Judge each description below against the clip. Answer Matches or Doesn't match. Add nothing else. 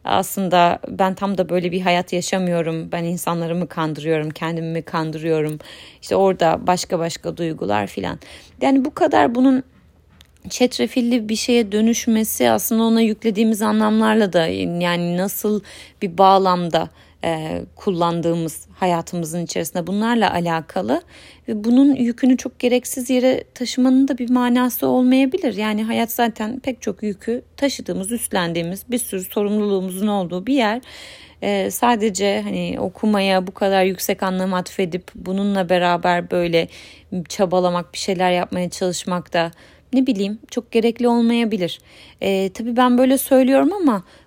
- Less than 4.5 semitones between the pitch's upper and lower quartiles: Doesn't match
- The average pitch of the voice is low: Doesn't match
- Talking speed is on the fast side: Doesn't match